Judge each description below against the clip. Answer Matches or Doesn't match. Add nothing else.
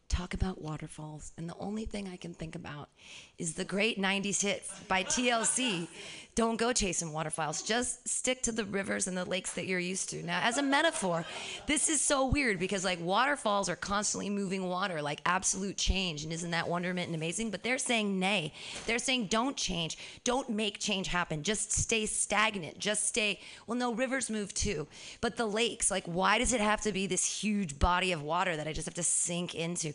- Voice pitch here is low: Doesn't match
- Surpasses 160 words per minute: Matches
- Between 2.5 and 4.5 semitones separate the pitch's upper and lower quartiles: Matches